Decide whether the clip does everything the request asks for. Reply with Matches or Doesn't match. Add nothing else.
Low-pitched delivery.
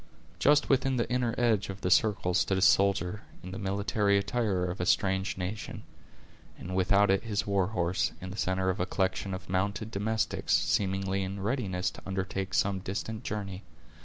Matches